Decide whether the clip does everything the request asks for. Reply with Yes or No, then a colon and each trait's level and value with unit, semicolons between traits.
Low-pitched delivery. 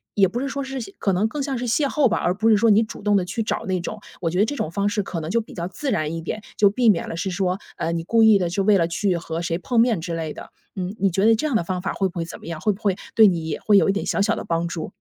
No: high, 195 Hz